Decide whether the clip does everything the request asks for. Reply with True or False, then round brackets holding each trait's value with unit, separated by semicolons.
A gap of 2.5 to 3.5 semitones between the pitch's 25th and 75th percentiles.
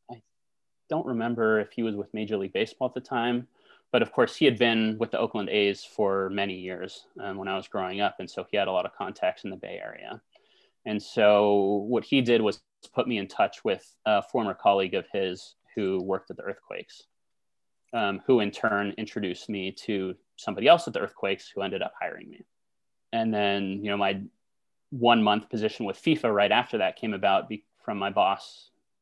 True (3.1 semitones)